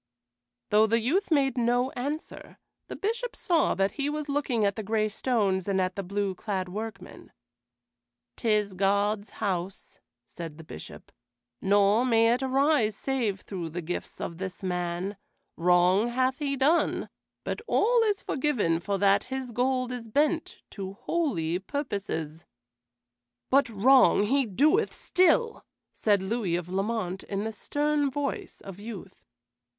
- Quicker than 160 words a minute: No, average, 145 wpm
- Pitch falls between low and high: No, high, 220 Hz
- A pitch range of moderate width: No, wide, 5.8 semitones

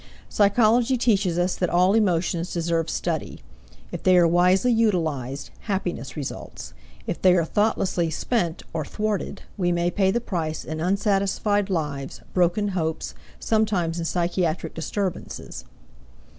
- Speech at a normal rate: No, slow, 130 wpm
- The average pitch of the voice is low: No, medium, 180 Hz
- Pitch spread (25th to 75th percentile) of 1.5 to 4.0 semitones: Yes, average, 3.6 semitones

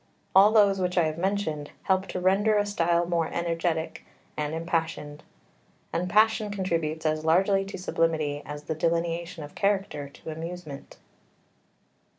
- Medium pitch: Yes, medium, 170 Hz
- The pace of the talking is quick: No, average, 145 wpm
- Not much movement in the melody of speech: No, average, 3.4 semitones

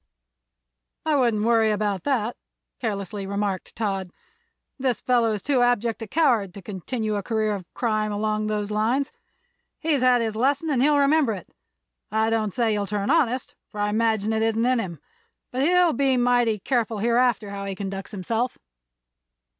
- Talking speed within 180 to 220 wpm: No, average, 170 wpm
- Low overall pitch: No, high, 225 Hz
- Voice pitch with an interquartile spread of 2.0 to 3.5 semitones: Yes, average, 3.2 semitones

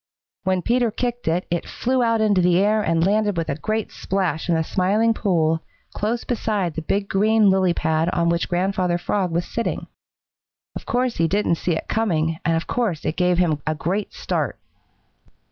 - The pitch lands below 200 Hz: Yes, medium, 185 Hz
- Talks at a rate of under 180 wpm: No, average, 190 wpm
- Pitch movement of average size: Yes, average, 4.4 semitones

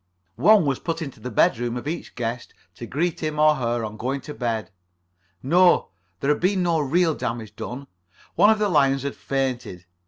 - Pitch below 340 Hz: Yes, medium, 140 Hz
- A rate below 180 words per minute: No, average, 190 wpm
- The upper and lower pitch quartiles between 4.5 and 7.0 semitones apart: Yes, average, 5.3 semitones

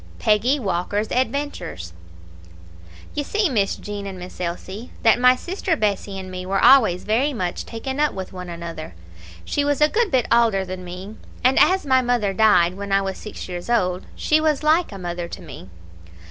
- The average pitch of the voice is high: Yes, high, 210 Hz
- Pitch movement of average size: No, wide, 6.4 semitones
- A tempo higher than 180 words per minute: Yes, average, 190 wpm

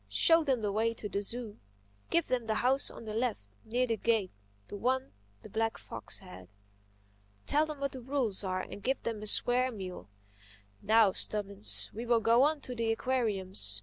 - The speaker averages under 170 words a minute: No, average, 180 wpm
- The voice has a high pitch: Yes, high, 225 Hz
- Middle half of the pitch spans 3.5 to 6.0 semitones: Yes, average, 4.5 semitones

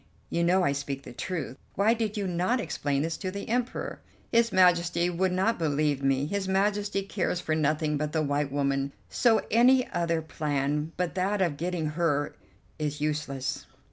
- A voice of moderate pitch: Yes, medium, 170 Hz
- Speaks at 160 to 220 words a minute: Yes, average, 175 wpm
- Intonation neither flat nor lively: Yes, average, 4.6 semitones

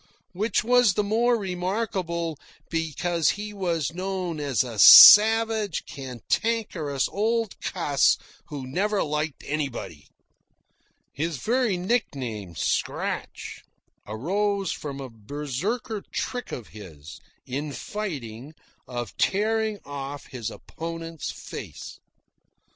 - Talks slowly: Yes, slow, 100 wpm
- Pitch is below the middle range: No, medium, 165 Hz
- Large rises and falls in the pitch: Yes, wide, 7.2 semitones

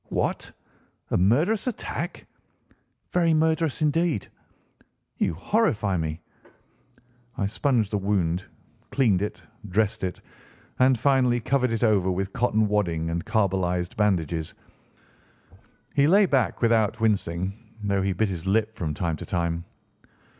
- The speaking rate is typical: No, slow, 125 wpm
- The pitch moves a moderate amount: No, wide, 5.9 semitones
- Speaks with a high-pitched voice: No, low, 105 Hz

